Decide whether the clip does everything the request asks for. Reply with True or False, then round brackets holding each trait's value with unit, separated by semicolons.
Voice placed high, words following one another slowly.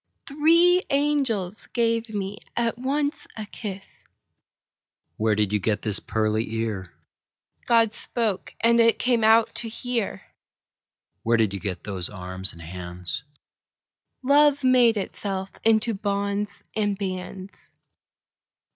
True (205 Hz; 110 wpm)